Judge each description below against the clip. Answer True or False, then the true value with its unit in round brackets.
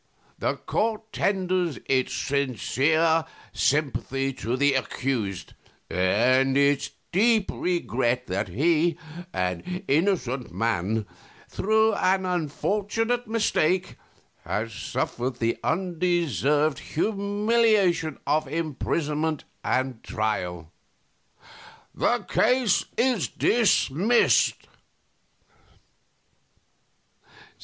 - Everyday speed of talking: False (75 wpm)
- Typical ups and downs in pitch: False (6.9 semitones)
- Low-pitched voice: False (155 Hz)